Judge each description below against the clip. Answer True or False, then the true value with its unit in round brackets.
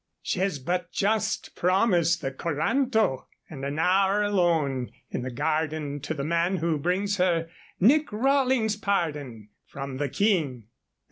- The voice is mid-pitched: True (170 Hz)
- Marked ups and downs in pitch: True (5.7 semitones)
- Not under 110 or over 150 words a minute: True (140 wpm)